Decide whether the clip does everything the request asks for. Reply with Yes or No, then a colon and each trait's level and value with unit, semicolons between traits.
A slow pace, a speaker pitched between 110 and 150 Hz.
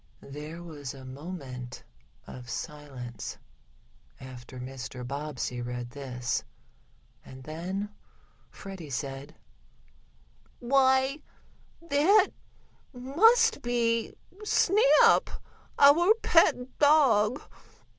No: slow, 75 wpm; medium, 165 Hz